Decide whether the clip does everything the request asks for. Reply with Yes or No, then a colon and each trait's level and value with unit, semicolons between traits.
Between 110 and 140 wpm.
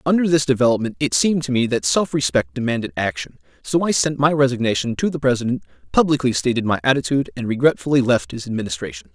No: average, 190 wpm